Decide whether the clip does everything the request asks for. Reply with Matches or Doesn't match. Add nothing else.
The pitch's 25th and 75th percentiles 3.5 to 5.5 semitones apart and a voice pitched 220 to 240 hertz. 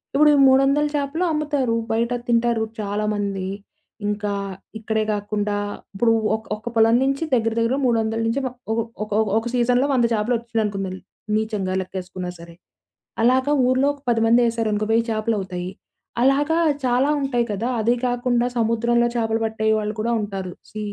Doesn't match